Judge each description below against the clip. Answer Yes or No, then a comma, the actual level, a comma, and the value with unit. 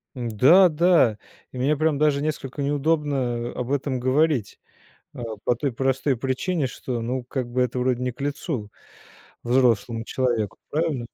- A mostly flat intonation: No, average, 3.3 semitones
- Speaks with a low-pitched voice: Yes, low, 130 Hz